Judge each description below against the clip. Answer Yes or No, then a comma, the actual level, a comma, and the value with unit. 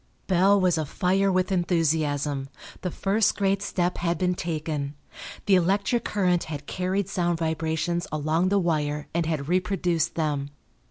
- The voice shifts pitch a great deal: No, average, 3.1 semitones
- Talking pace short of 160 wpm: Yes, average, 145 wpm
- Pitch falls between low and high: Yes, medium, 175 Hz